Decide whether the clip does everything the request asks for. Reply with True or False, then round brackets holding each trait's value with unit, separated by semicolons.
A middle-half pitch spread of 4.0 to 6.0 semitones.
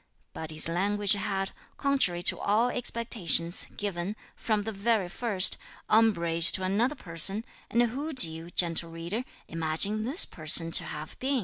True (5.2 semitones)